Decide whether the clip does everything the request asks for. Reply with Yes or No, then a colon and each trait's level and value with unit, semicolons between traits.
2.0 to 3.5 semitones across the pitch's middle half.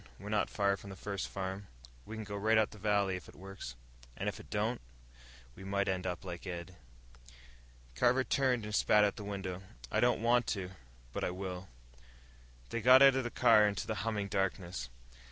Yes: narrow, 2.6 semitones